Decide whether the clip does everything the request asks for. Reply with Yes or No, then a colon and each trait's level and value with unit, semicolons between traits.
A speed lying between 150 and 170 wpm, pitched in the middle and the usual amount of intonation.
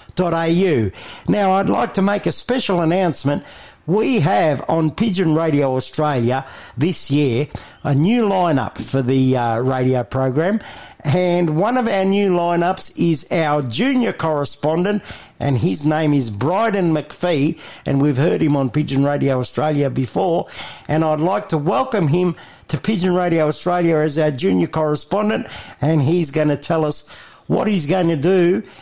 Yes: average, 155 wpm; medium, 160 Hz; average, 4.2 semitones